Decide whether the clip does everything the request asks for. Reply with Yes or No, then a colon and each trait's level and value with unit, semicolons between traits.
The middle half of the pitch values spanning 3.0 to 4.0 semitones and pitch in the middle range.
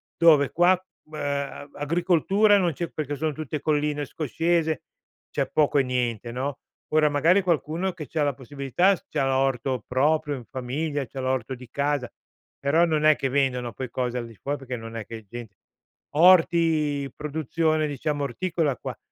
Yes: average, 3.5 semitones; medium, 145 Hz